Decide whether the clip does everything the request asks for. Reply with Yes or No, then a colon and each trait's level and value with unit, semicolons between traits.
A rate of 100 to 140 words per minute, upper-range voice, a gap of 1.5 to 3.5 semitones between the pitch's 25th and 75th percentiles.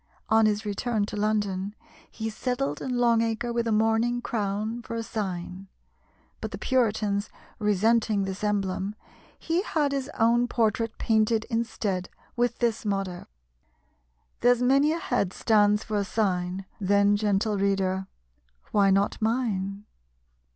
Yes: slow, 135 wpm; high, 215 Hz; average, 2.8 semitones